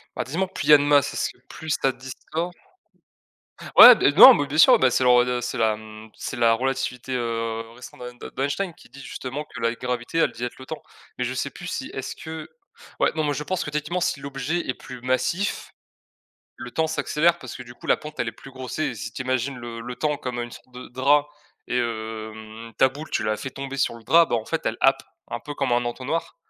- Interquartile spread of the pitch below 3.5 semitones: No, average, 3.8 semitones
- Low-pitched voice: Yes, low, 130 Hz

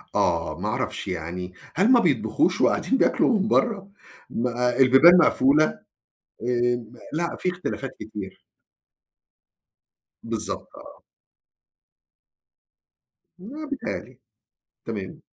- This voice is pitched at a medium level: No, low, 130 Hz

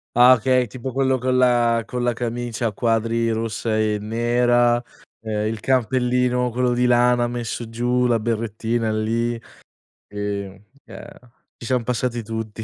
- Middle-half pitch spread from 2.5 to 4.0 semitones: No, narrow, 1.7 semitones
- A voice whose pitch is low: Yes, low, 120 Hz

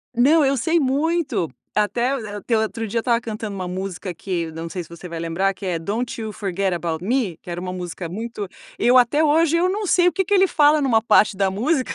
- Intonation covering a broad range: Yes, wide, 7.0 semitones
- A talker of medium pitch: No, high, 220 Hz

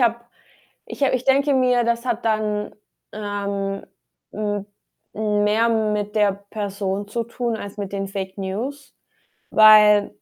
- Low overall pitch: No, high, 210 Hz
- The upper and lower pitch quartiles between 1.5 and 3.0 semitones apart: Yes, narrow, 2.5 semitones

